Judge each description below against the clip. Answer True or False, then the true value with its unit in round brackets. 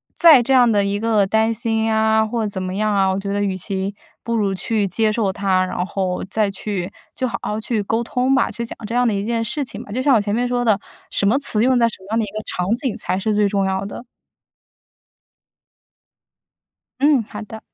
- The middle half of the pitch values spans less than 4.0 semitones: True (2.8 semitones)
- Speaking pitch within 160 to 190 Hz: False (215 Hz)